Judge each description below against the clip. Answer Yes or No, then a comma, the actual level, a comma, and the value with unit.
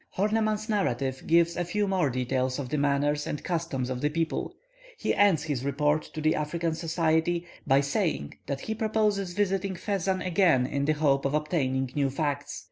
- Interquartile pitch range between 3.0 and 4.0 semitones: No, average, 4.8 semitones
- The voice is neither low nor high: Yes, medium, 155 Hz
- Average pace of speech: Yes, average, 180 wpm